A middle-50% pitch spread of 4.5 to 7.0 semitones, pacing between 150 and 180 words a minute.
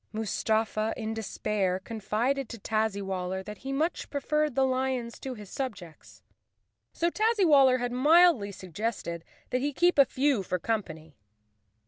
No: average, 5.2 semitones; average, 140 wpm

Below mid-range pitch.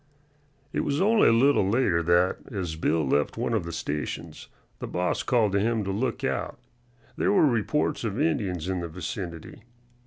Yes: low, 100 Hz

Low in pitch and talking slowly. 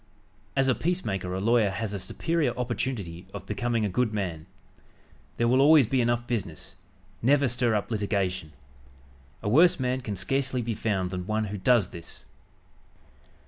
No: low, 115 Hz; average, 160 wpm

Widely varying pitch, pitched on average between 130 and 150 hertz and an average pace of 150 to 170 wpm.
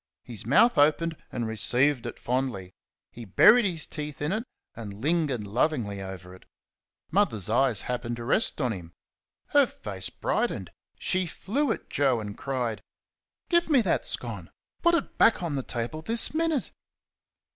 Yes: wide, 8.3 semitones; low, 135 Hz; average, 155 wpm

